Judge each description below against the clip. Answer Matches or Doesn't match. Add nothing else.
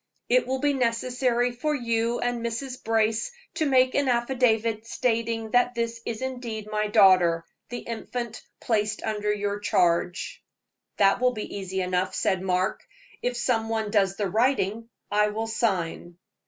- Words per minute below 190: Matches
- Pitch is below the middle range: Doesn't match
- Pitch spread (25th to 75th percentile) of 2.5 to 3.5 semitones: Matches